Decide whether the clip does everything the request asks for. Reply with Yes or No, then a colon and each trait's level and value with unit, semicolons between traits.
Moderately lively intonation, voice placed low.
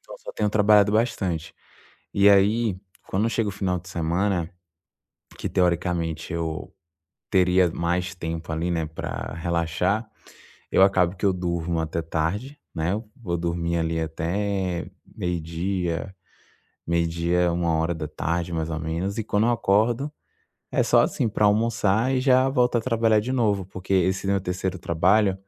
Yes: average, 3.5 semitones; very low, 90 Hz